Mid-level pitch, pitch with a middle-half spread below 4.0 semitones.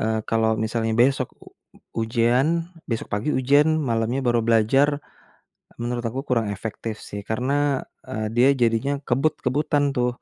No: low, 120 Hz; average, 2.7 semitones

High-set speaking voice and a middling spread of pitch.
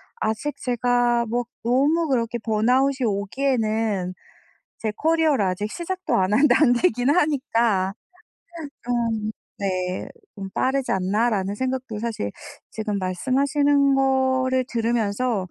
Yes: high, 240 Hz; average, 4.2 semitones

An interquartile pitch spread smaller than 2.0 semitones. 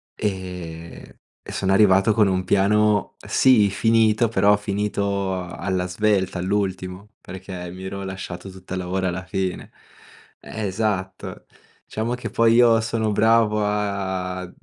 No: narrow, 2.3 semitones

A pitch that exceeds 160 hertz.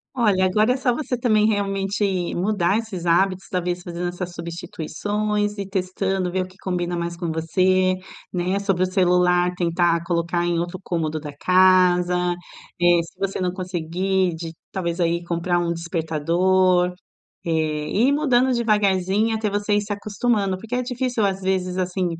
Yes: medium, 185 Hz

